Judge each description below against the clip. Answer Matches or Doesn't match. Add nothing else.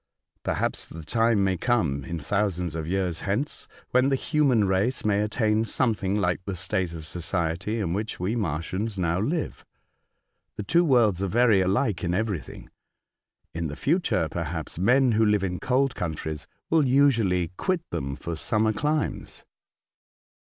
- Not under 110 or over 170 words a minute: Matches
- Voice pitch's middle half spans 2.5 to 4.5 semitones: Doesn't match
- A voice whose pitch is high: Doesn't match